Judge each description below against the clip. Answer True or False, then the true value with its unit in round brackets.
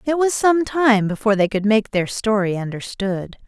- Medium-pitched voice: False (220 Hz)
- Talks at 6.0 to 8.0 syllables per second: False (4.9 syllables/s)